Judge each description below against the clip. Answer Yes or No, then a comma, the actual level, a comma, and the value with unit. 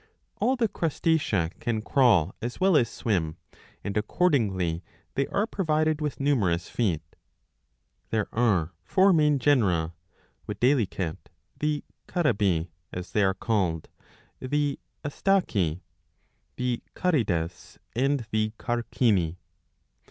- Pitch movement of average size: No, wide, 8.0 semitones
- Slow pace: Yes, slow, 110 wpm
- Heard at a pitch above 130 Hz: No, low, 115 Hz